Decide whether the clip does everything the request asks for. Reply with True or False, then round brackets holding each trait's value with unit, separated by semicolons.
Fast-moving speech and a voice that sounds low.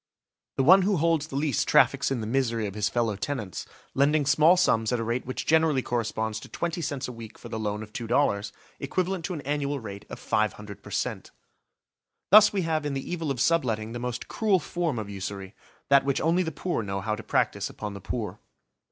True (220 wpm; 130 Hz)